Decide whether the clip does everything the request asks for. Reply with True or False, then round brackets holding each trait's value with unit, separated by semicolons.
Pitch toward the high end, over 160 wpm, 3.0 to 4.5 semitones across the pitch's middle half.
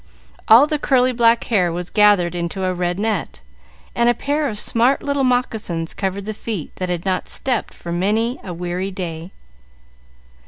False (200 Hz; 170 wpm; 5.0 semitones)